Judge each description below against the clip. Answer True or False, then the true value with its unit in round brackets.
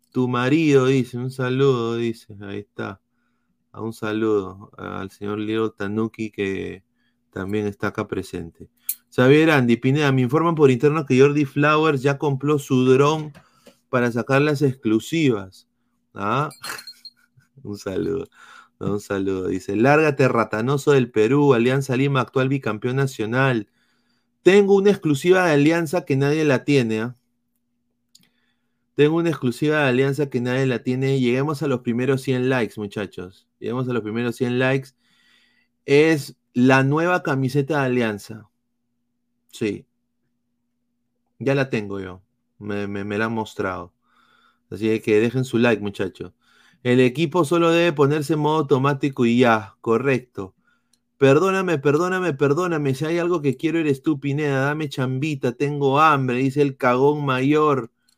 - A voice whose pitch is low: True (130 Hz)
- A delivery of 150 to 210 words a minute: False (140 wpm)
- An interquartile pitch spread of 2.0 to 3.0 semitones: False (4.1 semitones)